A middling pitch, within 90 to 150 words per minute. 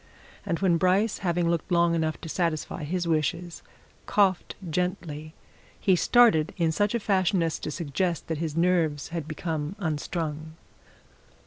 Yes: medium, 170 Hz; average, 145 wpm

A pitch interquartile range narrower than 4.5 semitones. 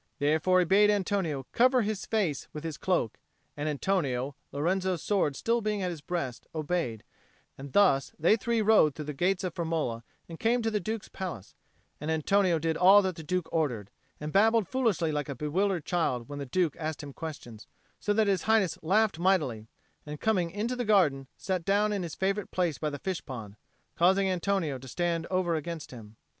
No: average, 5.0 semitones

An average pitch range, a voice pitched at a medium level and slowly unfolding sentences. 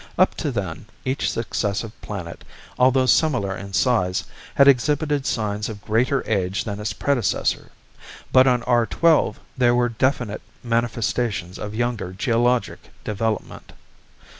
No: average, 3.7 semitones; low, 115 Hz; slow, 130 wpm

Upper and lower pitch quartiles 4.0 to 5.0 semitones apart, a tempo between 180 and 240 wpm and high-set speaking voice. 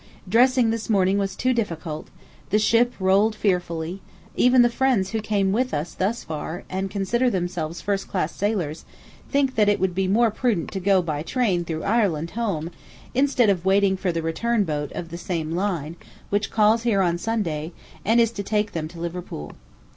Yes: average, 4.7 semitones; average, 185 wpm; high, 195 Hz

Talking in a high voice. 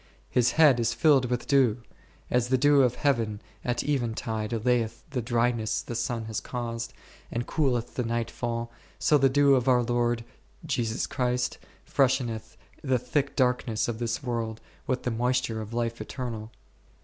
No: low, 120 Hz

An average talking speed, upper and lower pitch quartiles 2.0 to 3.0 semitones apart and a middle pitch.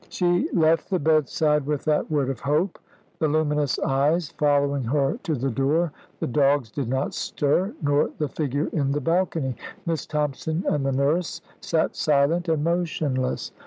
Yes: average, 160 wpm; average, 2.7 semitones; medium, 150 Hz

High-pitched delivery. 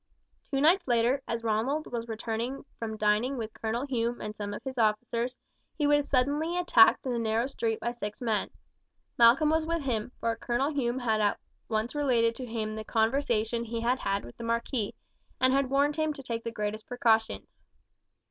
Yes: high, 235 Hz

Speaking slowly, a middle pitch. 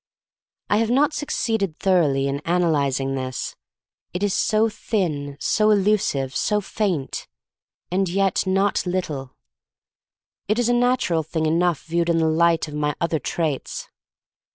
No: average, 155 wpm; medium, 170 Hz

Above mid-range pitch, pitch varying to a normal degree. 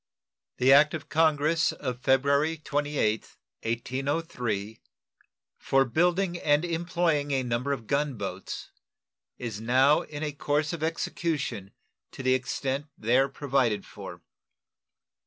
No: medium, 140 Hz; average, 3.7 semitones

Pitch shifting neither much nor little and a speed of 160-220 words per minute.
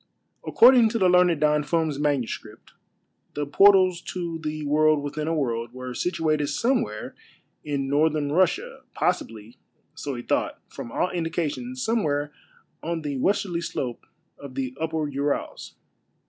No: average, 3.3 semitones; slow, 135 wpm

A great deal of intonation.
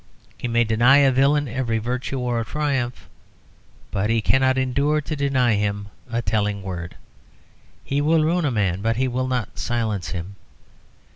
No: average, 4.1 semitones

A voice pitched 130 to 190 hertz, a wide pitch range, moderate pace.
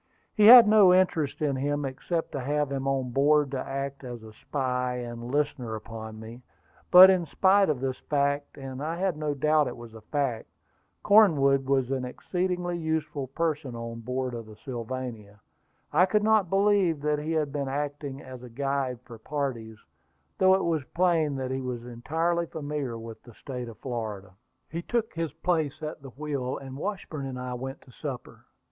No: medium, 140 Hz; average, 4.1 semitones; average, 190 wpm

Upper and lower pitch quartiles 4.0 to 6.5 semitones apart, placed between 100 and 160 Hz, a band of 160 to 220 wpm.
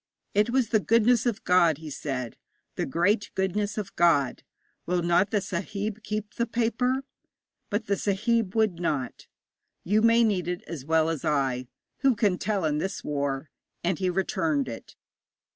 No: average, 5.1 semitones; high, 190 Hz; average, 165 wpm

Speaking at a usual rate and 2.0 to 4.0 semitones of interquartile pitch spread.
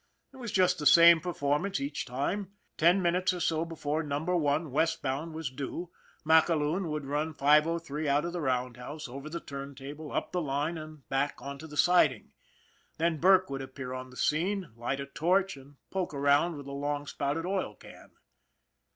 Yes: average, 175 wpm; average, 3.4 semitones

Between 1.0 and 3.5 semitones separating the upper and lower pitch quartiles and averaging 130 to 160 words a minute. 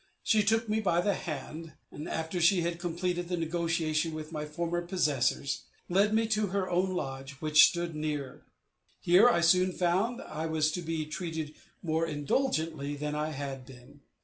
No: average, 2.9 semitones; average, 175 wpm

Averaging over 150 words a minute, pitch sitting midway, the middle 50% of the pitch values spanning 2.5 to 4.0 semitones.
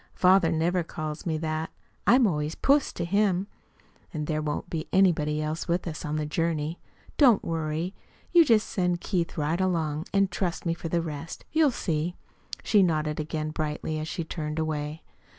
Yes: average, 180 wpm; medium, 165 Hz; average, 2.9 semitones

